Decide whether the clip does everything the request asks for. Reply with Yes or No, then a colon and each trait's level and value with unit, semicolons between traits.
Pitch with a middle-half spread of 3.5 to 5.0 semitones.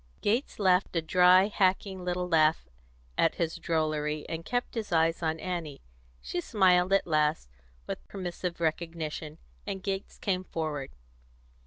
No: average, 2.9 semitones